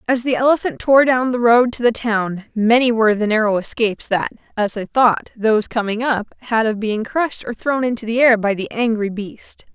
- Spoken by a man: No, female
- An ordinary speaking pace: No, fast, 215 wpm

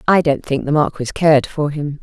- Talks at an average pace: No, fast, 235 wpm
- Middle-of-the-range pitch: Yes, medium, 150 Hz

